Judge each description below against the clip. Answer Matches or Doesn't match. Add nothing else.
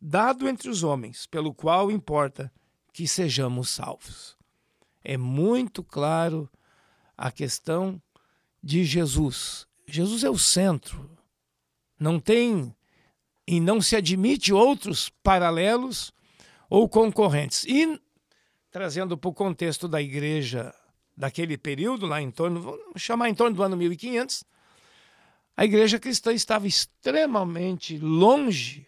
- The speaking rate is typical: Doesn't match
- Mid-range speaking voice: Matches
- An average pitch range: Doesn't match